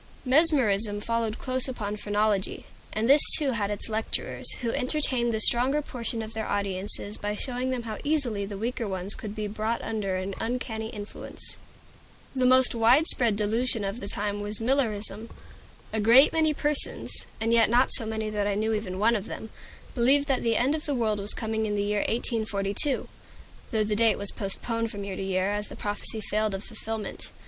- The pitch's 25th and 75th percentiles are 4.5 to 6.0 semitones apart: No, average, 2.9 semitones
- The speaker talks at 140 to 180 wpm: No, average, 190 wpm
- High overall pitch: Yes, high, 220 Hz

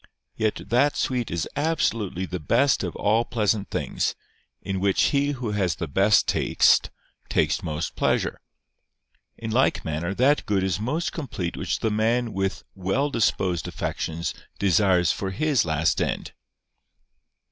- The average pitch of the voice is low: Yes, low, 105 Hz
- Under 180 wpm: Yes, average, 145 wpm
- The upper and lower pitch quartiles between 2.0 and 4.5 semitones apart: No, average, 5.1 semitones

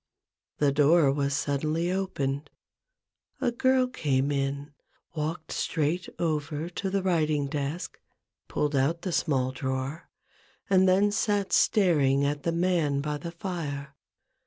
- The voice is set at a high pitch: No, medium, 155 Hz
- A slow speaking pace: Yes, slow, 130 wpm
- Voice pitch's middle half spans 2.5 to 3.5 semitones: No, average, 4.1 semitones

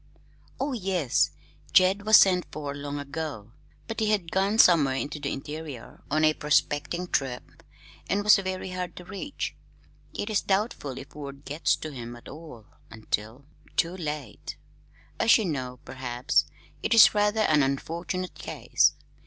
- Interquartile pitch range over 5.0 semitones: Yes, wide, 5.6 semitones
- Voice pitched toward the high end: No, medium, 155 Hz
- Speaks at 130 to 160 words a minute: Yes, average, 155 wpm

